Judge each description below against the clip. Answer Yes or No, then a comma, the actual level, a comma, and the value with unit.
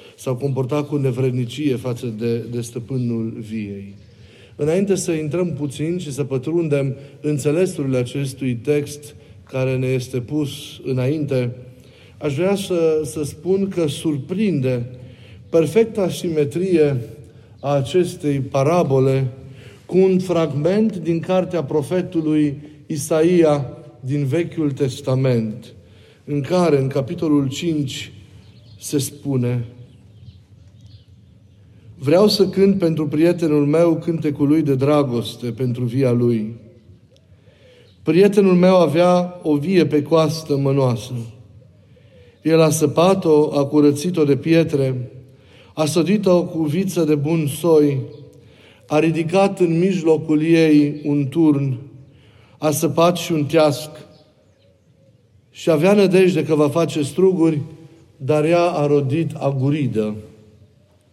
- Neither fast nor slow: No, slow, 110 wpm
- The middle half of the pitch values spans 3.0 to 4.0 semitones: No, average, 4.6 semitones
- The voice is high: No, medium, 145 Hz